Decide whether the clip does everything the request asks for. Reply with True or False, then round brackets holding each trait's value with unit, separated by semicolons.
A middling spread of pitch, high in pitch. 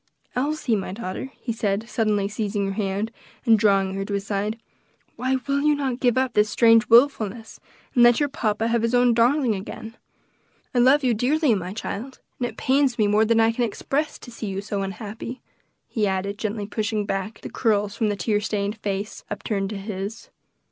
True (3.2 semitones; 220 Hz)